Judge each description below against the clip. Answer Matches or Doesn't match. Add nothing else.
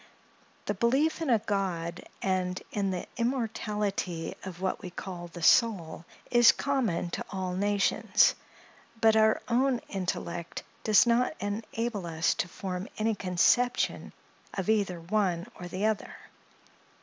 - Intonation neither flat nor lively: Matches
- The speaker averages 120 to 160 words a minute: Matches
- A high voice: Matches